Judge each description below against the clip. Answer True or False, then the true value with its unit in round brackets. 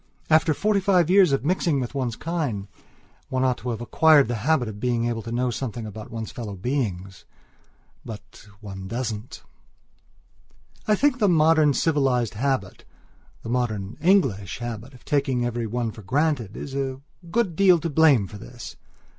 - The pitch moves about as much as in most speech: False (5.7 semitones)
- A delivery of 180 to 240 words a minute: False (160 wpm)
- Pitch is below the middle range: True (125 Hz)